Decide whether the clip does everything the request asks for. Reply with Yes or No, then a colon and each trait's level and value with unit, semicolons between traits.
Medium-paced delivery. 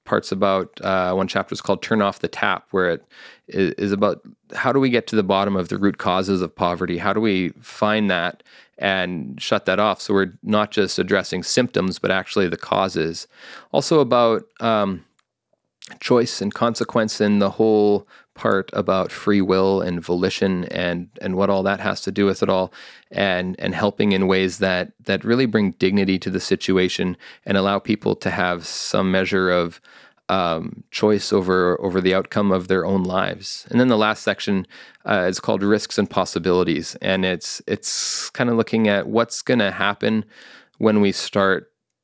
Yes: average, 185 wpm